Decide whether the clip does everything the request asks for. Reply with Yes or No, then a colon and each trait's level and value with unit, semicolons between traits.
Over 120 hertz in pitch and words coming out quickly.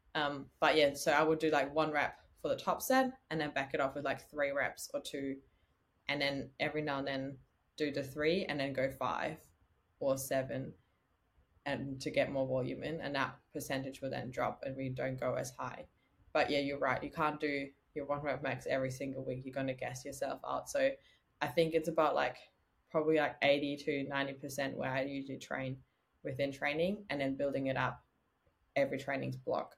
Yes: medium, 140 Hz; fast, 210 wpm